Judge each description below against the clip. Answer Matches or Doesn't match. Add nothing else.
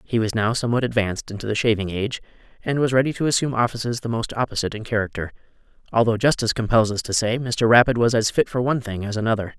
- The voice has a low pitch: Matches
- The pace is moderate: Doesn't match